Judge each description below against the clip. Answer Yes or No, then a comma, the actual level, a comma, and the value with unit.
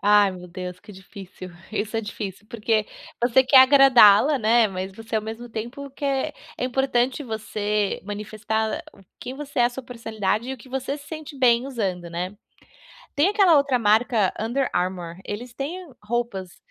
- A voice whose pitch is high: Yes, high, 225 Hz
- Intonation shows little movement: No, average, 4.4 semitones